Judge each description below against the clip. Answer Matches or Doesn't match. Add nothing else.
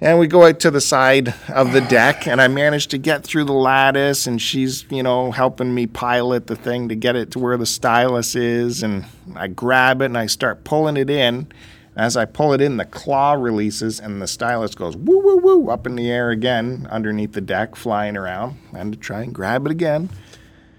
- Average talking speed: Doesn't match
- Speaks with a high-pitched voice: Doesn't match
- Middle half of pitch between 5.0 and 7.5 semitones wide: Doesn't match